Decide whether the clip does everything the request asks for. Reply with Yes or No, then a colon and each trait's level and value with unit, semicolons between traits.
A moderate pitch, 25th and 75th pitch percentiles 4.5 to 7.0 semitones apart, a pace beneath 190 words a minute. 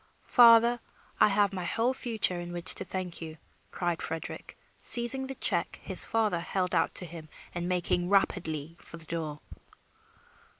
Yes: medium, 180 Hz; average, 5.0 semitones; average, 160 wpm